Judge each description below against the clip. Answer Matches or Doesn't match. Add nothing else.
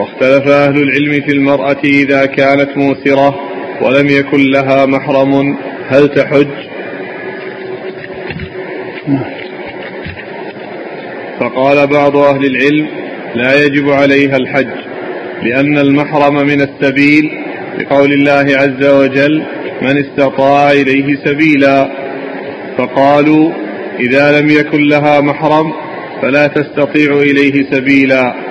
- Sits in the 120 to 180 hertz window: Matches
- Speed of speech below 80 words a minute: Doesn't match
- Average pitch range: Doesn't match